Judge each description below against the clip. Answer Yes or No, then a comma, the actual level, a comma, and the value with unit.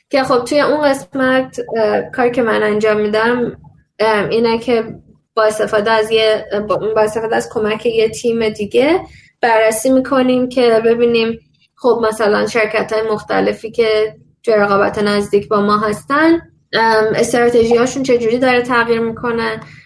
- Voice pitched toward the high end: Yes, high, 225 Hz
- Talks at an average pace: Yes, average, 135 wpm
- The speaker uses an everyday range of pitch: No, narrow, 2.2 semitones